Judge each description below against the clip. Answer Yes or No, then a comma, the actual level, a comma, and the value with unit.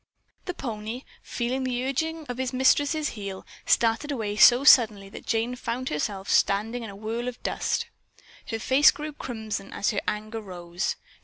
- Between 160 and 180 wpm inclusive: Yes, average, 165 wpm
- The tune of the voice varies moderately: Yes, average, 3.7 semitones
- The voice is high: Yes, high, 235 Hz